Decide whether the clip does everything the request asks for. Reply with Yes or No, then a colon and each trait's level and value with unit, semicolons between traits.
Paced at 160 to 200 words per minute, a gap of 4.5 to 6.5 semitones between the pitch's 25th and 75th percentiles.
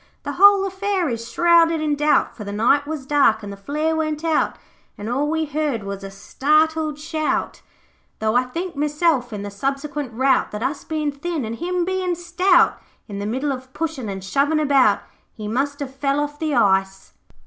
Yes: average, 190 wpm; average, 4.9 semitones